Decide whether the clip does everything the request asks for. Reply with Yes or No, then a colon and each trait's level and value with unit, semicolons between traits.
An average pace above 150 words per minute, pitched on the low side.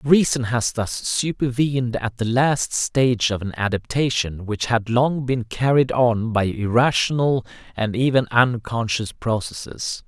No: slow, 135 wpm; low, 120 Hz